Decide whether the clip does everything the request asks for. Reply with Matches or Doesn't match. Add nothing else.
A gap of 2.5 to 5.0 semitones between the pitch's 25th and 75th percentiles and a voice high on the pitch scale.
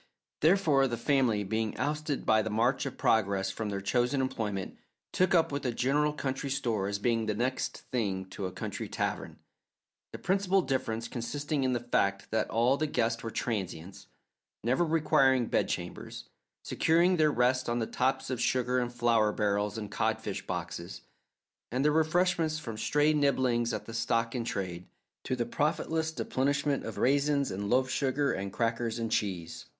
Doesn't match